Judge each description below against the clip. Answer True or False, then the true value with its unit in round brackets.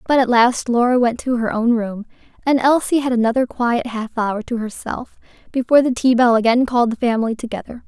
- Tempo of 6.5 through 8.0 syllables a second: False (5.7 syllables/s)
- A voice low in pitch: False (240 Hz)